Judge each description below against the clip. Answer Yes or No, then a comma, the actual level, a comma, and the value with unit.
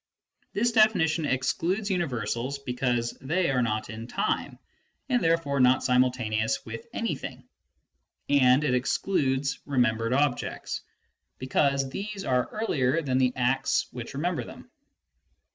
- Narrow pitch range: No, average, 4.8 semitones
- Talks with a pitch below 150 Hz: Yes, low, 135 Hz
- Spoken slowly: Yes, slow, 125 wpm